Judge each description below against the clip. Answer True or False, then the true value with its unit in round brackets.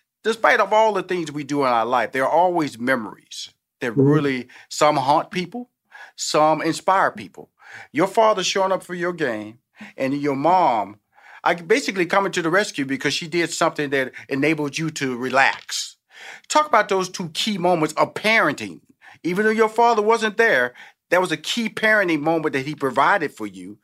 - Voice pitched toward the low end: False (160 Hz)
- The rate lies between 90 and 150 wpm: False (180 wpm)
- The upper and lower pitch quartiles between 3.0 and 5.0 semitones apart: False (5.6 semitones)